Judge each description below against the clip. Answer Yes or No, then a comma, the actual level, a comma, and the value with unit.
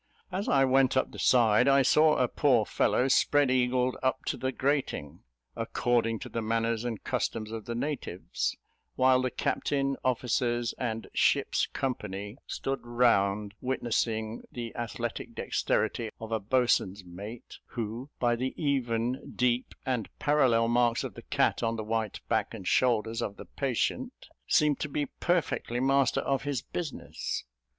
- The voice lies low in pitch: Yes, low, 120 Hz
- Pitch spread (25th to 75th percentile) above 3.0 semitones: No, average, 2.7 semitones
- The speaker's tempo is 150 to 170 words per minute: Yes, average, 155 wpm